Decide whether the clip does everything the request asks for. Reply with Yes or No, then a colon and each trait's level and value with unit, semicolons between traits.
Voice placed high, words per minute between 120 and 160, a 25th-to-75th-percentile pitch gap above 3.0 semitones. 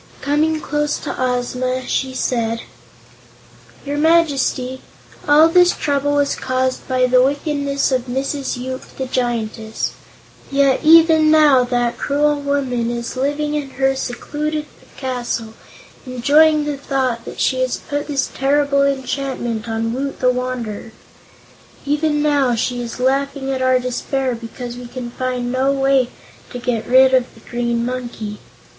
No: very high, 260 Hz; average, 140 wpm; narrow, 2.5 semitones